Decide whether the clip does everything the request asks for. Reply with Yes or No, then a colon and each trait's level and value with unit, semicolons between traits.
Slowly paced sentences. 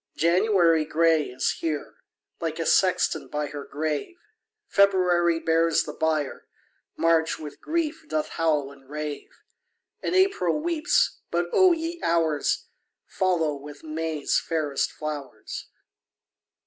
Yes: slow, 125 wpm